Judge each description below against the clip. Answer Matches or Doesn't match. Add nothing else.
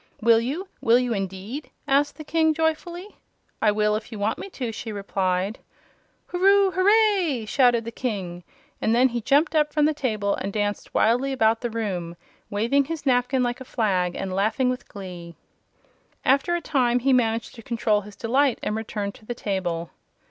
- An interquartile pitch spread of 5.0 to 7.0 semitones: Matches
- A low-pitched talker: Doesn't match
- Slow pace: Doesn't match